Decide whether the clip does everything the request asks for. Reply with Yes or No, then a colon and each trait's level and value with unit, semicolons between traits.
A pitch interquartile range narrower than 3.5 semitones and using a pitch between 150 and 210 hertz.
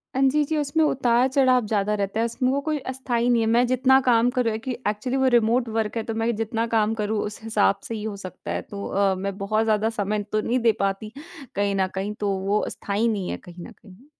No: average, 3.1 semitones; high, 220 Hz